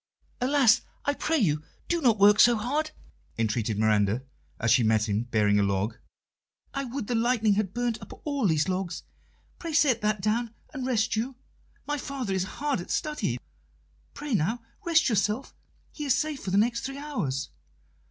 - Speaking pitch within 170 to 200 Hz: No, high, 220 Hz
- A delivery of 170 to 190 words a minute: Yes, average, 175 wpm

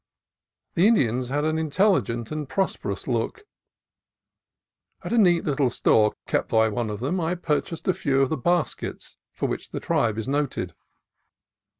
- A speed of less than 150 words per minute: No, average, 160 wpm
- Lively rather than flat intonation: Yes, wide, 6.2 semitones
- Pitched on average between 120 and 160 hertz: Yes, medium, 140 Hz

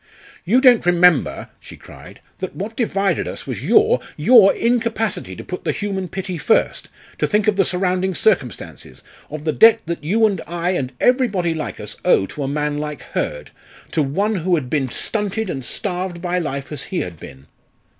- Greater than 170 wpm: Yes, average, 185 wpm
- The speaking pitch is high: No, medium, 180 Hz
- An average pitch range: No, wide, 5.8 semitones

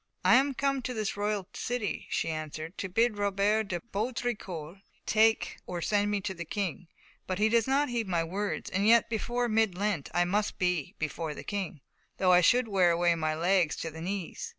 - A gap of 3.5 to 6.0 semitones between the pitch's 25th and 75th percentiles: Yes, average, 4.1 semitones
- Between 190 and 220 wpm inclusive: Yes, average, 200 wpm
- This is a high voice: Yes, high, 200 Hz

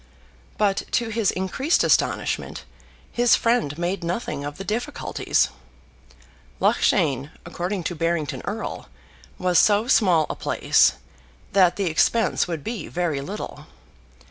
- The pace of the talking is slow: Yes, slow, 120 wpm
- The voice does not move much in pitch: No, average, 4.5 semitones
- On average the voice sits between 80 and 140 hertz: No, medium, 185 Hz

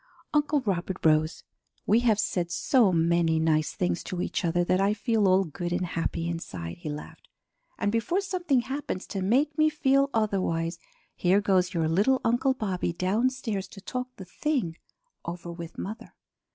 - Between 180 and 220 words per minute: No, average, 165 wpm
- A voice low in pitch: No, high, 190 Hz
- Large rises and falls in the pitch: Yes, wide, 6.0 semitones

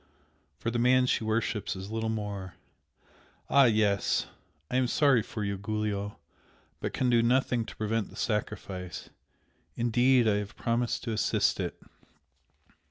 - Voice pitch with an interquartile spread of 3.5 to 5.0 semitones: No, average, 2.8 semitones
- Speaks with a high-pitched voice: No, low, 110 Hz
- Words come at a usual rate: Yes, average, 145 wpm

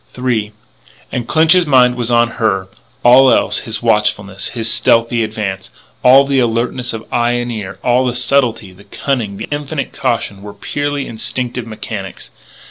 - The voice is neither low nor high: No, low, 120 Hz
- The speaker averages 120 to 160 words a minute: Yes, average, 155 wpm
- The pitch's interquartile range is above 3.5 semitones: No, average, 2.8 semitones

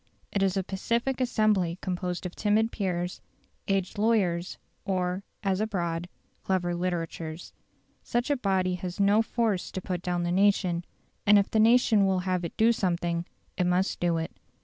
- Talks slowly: No, average, 165 wpm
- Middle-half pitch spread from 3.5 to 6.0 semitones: No, average, 2.9 semitones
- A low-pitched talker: No, medium, 185 Hz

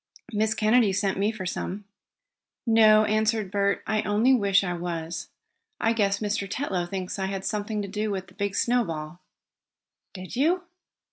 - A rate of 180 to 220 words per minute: No, average, 160 wpm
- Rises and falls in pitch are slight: Yes, narrow, 2.3 semitones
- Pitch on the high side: Yes, high, 205 Hz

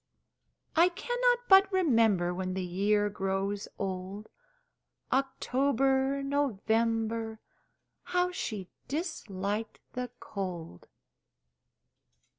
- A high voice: Yes, high, 225 Hz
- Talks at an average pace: No, slow, 80 wpm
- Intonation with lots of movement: Yes, wide, 6.3 semitones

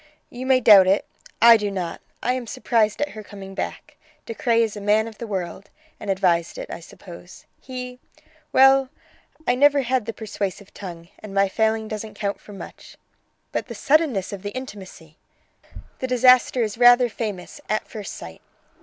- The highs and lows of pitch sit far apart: No, average, 4.1 semitones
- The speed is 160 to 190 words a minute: Yes, average, 180 wpm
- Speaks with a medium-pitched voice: No, high, 215 Hz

